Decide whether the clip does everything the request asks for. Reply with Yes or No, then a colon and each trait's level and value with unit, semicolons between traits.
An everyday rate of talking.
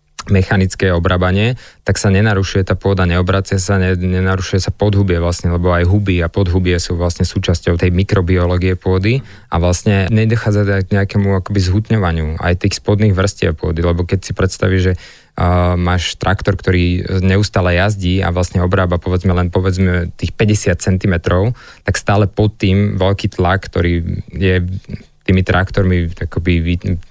Yes: average, 150 wpm